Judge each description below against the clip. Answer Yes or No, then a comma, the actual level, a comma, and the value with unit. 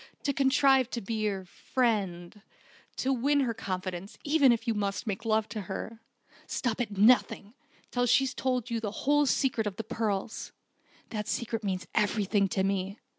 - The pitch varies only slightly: No, average, 4.0 semitones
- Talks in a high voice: Yes, high, 220 Hz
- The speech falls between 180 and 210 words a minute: No, average, 170 wpm